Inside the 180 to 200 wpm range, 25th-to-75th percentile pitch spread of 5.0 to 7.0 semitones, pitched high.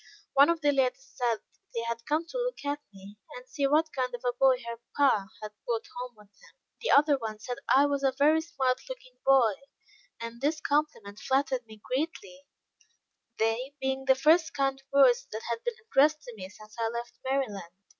No: average, 195 wpm; average, 3.8 semitones; very high, 265 Hz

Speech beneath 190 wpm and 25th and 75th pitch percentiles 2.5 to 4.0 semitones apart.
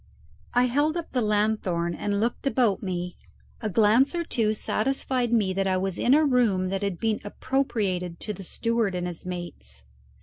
No: average, 180 wpm; average, 4.8 semitones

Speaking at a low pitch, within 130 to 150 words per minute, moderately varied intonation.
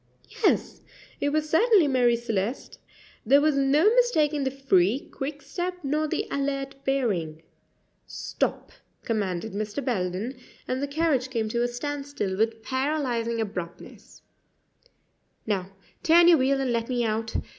No: very high, 260 Hz; slow, 135 wpm; average, 4.4 semitones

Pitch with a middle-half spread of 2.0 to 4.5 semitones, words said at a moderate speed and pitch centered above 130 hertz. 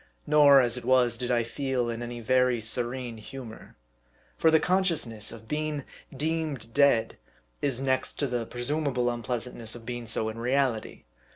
No: average, 3.1 semitones; average, 160 wpm; low, 125 Hz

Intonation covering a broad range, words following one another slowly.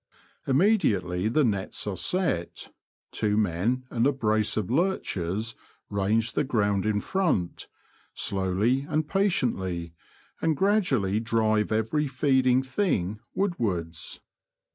Yes: wide, 6.1 semitones; slow, 115 wpm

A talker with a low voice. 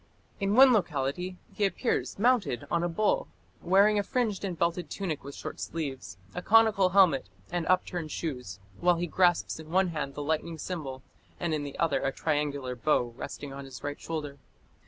No: medium, 165 Hz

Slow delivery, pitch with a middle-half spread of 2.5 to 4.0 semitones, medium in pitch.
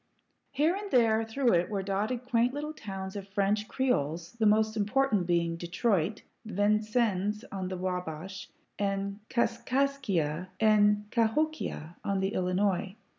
No: slow, 130 wpm; average, 3.7 semitones; high, 205 Hz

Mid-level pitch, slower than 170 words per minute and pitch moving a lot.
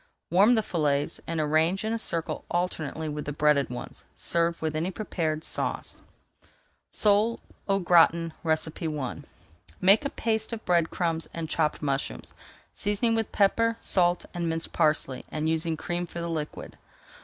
No: medium, 170 Hz; average, 160 wpm; average, 3.8 semitones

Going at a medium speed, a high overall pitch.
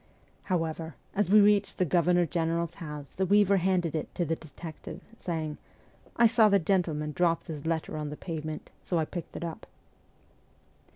No: average, 175 wpm; medium, 170 Hz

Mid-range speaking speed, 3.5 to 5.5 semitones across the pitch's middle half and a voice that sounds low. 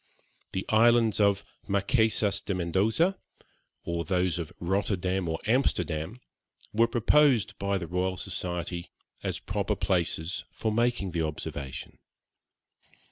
No: slow, 115 wpm; average, 4.0 semitones; very low, 95 Hz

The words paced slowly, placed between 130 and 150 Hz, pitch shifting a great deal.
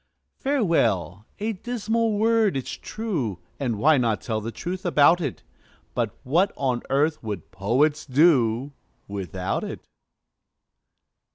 Yes: slow, 120 wpm; medium, 140 Hz; wide, 9.0 semitones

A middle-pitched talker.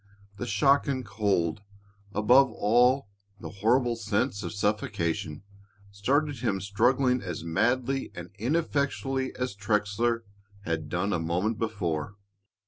No: low, 105 Hz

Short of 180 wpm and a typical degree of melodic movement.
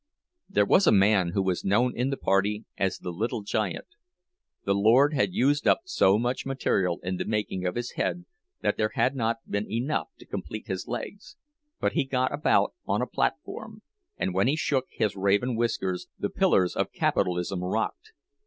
No: average, 185 wpm; average, 5.0 semitones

